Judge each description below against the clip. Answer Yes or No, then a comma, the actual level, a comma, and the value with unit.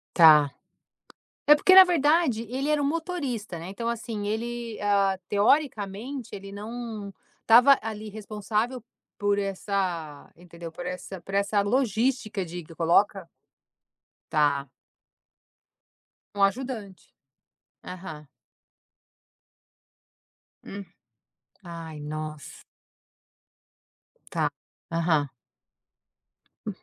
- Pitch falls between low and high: No, high, 205 Hz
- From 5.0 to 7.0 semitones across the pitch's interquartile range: Yes, wide, 5.4 semitones